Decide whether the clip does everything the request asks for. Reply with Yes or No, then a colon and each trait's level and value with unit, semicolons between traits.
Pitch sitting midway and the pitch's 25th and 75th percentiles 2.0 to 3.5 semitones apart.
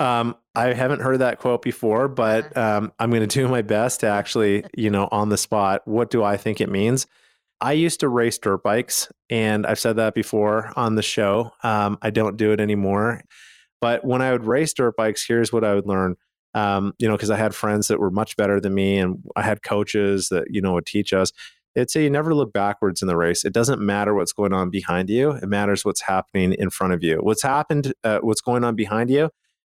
No: low, 110 Hz; average, 2.9 semitones